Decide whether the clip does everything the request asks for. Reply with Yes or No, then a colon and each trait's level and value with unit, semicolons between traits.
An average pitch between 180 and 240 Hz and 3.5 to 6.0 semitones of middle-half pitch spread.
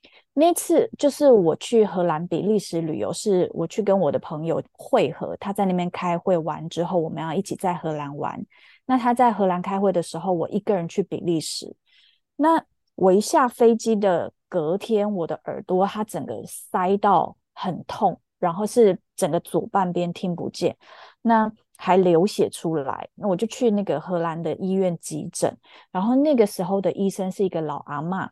Yes: high, 190 Hz; average, 3.9 semitones